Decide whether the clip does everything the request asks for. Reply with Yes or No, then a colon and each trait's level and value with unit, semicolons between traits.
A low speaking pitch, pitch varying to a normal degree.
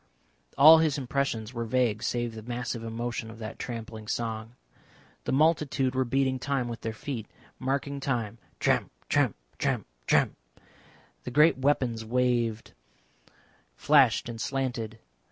Yes: low, 120 Hz; average, 3.0 semitones